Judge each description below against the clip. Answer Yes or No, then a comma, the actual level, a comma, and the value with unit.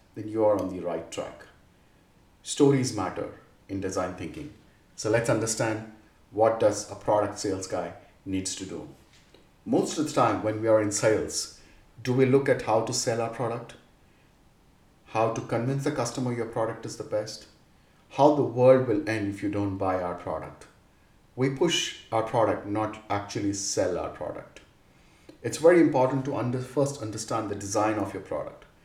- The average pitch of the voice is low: Yes, low, 110 Hz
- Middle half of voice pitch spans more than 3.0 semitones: Yes, average, 3.8 semitones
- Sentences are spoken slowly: No, average, 175 wpm